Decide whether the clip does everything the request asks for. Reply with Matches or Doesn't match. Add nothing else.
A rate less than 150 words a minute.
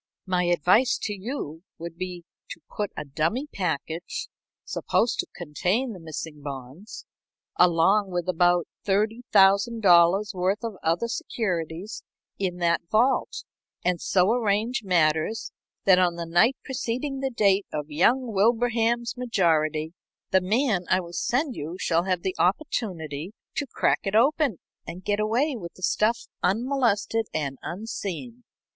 Matches